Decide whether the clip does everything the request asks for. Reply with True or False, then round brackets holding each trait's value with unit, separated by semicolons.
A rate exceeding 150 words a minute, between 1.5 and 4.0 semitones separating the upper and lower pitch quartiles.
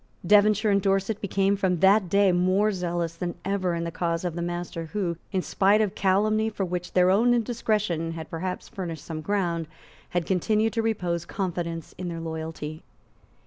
True (180 wpm; 3.1 semitones)